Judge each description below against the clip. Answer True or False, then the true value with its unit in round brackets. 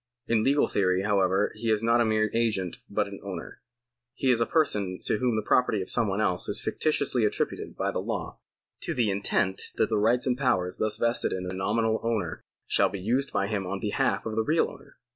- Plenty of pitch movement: False (3.2 semitones)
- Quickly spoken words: True (220 wpm)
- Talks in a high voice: False (110 Hz)